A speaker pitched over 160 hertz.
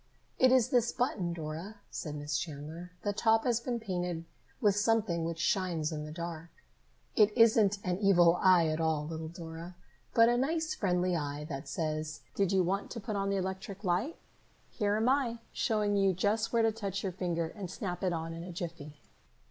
Yes: medium, 185 Hz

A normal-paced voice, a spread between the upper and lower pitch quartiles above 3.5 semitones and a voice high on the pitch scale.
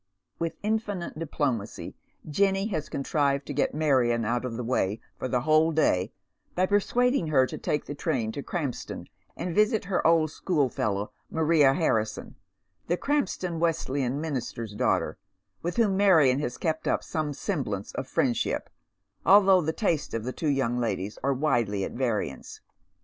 No: average, 155 wpm; wide, 5.6 semitones; medium, 150 Hz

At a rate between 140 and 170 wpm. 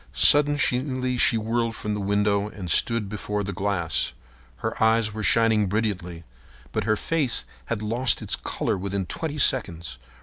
Yes: average, 155 wpm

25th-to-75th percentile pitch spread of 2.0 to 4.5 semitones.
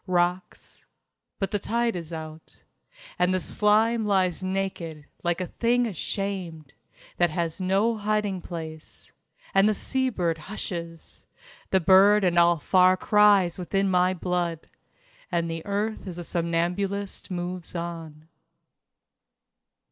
Yes: average, 3.0 semitones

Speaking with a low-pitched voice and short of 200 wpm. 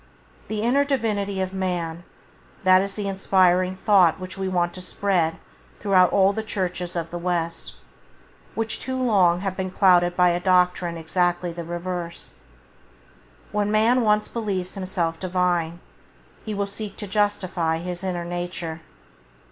No: medium, 185 Hz; average, 150 wpm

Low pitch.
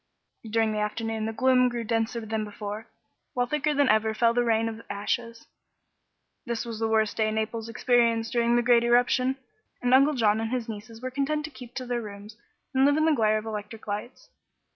No: high, 230 Hz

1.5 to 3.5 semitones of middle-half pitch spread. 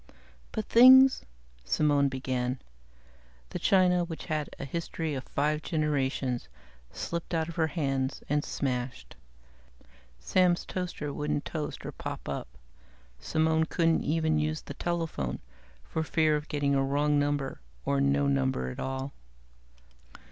Yes: average, 3.1 semitones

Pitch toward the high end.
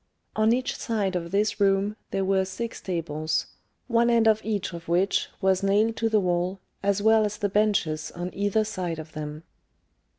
Yes: high, 195 Hz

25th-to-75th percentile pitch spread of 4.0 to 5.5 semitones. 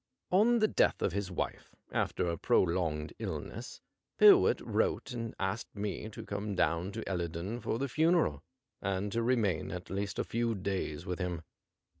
Yes: average, 4.6 semitones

